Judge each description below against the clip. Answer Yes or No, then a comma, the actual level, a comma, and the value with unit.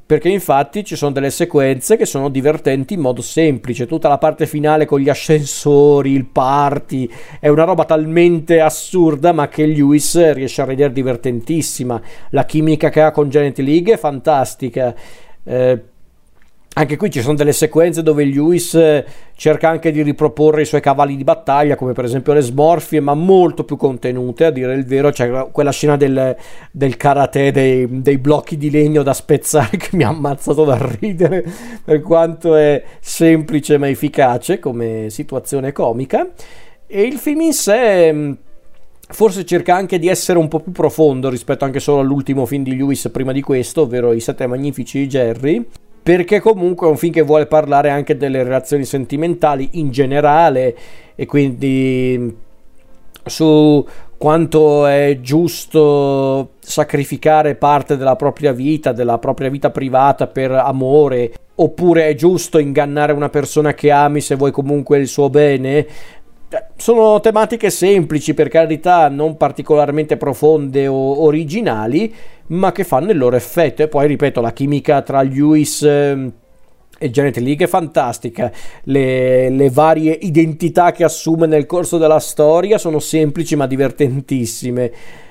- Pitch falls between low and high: Yes, medium, 150 Hz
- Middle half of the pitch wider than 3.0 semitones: No, average, 2.7 semitones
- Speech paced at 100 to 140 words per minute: No, average, 155 wpm